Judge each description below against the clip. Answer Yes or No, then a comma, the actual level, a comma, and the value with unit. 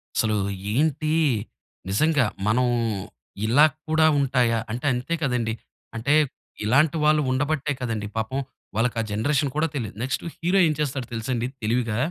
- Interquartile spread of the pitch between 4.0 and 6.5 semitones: Yes, average, 4.7 semitones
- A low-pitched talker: Yes, low, 130 Hz